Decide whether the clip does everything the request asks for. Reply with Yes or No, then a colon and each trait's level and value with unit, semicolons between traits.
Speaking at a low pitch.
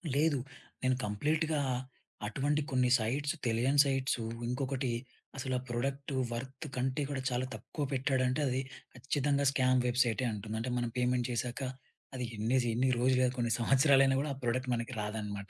Yes: low, 130 Hz